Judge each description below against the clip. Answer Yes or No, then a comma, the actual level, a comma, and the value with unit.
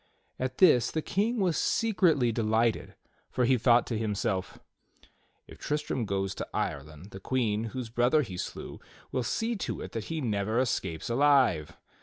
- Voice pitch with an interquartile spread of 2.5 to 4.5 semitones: No, wide, 5.4 semitones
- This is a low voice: Yes, low, 120 Hz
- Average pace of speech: Yes, average, 160 wpm